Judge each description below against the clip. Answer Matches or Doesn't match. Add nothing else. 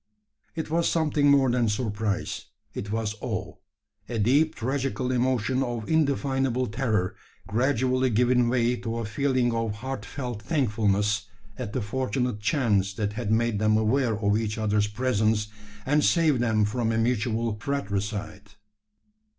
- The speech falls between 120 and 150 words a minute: Matches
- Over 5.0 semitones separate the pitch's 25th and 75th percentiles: Doesn't match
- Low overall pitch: Matches